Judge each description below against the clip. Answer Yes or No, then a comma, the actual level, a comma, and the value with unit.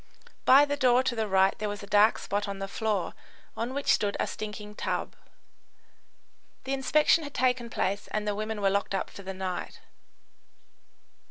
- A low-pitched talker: No, high, 210 Hz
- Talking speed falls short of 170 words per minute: No, average, 180 wpm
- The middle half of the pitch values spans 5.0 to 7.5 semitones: No, average, 4.1 semitones